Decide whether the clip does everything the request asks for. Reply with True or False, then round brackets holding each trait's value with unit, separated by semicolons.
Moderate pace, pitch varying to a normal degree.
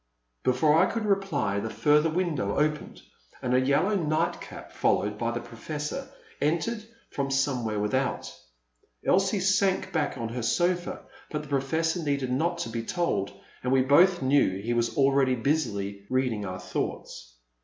False (155 wpm; 6.0 semitones)